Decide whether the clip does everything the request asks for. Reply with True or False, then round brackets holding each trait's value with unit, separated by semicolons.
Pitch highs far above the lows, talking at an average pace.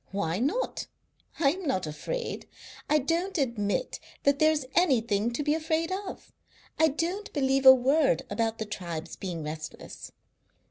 True (7.8 semitones; 150 wpm)